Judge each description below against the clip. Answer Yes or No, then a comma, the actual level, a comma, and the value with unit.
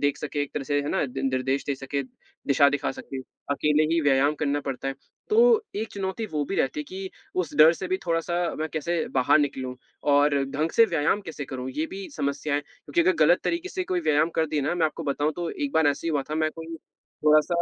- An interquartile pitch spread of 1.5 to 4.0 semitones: Yes, average, 3.3 semitones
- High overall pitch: No, medium, 150 Hz